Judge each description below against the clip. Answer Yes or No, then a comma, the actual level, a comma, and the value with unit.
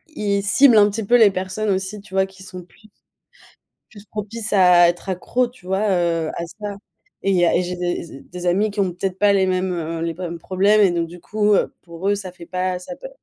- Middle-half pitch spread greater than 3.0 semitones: No, average, 2.7 semitones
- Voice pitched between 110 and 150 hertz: No, high, 190 Hz